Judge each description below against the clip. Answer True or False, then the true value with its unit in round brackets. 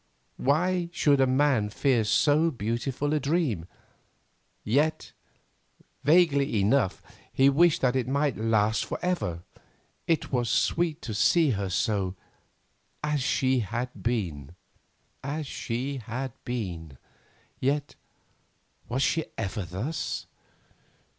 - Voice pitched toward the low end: True (130 Hz)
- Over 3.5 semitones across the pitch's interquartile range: True (5.3 semitones)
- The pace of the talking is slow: True (110 wpm)